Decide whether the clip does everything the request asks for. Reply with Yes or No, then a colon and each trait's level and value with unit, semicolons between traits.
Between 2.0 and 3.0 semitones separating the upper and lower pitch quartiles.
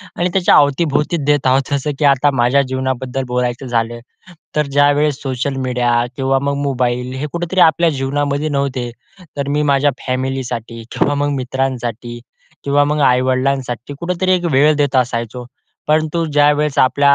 Yes: narrow, 2.4 semitones